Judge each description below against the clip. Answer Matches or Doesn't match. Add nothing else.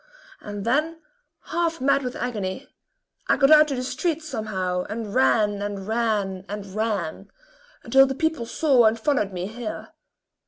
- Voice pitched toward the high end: Matches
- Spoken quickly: Doesn't match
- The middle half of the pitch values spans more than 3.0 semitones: Matches